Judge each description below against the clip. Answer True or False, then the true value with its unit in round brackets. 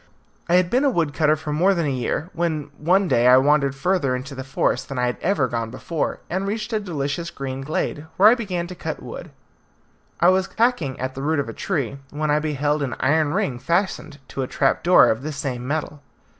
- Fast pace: True (225 wpm)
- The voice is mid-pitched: True (150 Hz)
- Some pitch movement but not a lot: True (4.7 semitones)